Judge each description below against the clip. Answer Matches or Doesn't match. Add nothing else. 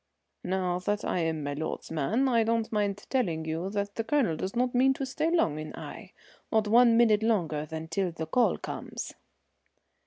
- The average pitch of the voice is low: Doesn't match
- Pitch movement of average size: Doesn't match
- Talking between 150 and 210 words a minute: Matches